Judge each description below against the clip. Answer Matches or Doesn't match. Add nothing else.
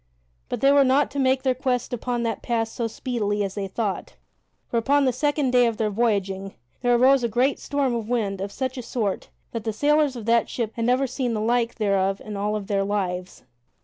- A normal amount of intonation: Matches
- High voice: Matches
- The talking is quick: Matches